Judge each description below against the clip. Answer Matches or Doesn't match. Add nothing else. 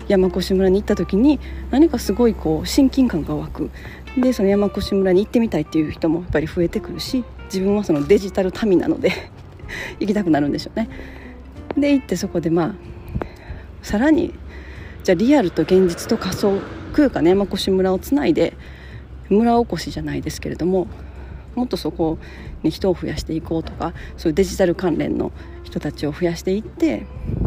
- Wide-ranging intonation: Matches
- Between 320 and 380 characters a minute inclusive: Matches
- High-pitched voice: Matches